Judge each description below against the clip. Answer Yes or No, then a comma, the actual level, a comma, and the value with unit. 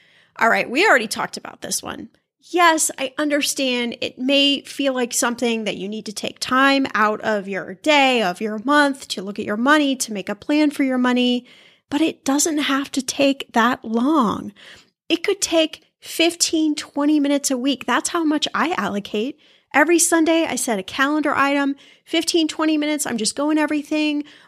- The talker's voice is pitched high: Yes, very high, 280 Hz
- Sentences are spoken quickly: No, average, 185 wpm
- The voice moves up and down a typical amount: Yes, average, 3.8 semitones